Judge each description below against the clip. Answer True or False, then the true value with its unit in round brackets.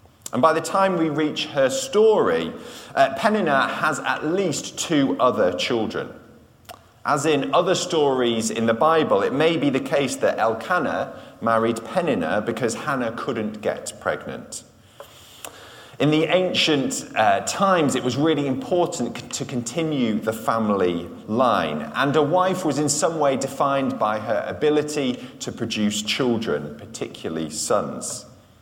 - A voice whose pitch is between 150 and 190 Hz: False (140 Hz)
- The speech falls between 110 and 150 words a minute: True (140 wpm)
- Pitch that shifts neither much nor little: False (6.5 semitones)